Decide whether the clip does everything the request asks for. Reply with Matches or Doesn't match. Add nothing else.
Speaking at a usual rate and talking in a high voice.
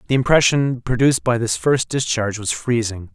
Doesn't match